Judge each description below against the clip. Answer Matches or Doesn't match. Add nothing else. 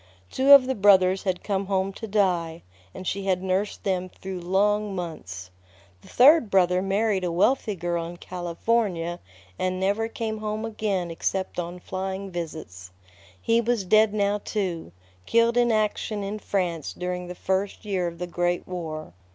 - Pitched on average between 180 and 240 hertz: Matches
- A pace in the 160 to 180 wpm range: Matches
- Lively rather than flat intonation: Doesn't match